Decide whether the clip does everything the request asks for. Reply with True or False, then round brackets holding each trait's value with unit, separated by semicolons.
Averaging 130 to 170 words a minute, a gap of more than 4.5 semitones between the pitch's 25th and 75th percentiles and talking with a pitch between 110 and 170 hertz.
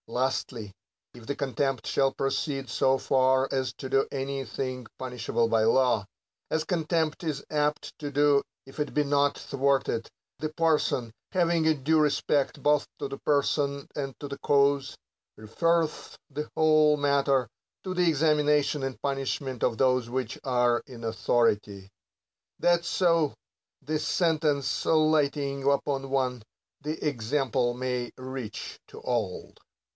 False (140 wpm; 2.7 semitones; 140 Hz)